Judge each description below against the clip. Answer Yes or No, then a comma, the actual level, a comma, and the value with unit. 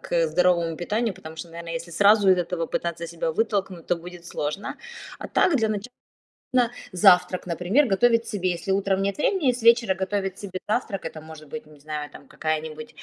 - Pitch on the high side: No, medium, 180 Hz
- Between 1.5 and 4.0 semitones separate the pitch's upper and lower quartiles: Yes, average, 3.7 semitones